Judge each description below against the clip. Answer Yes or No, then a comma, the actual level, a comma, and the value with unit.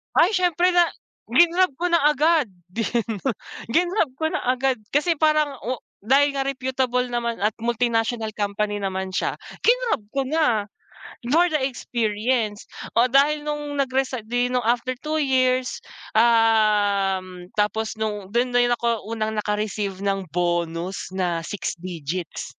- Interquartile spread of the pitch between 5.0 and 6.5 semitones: Yes, wide, 5.4 semitones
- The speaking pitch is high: Yes, high, 240 Hz